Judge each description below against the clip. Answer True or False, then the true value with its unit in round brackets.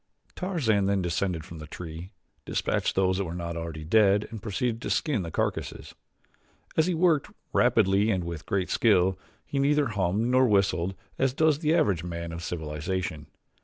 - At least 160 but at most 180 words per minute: True (170 wpm)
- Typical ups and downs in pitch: False (5.8 semitones)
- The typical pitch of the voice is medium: False (95 Hz)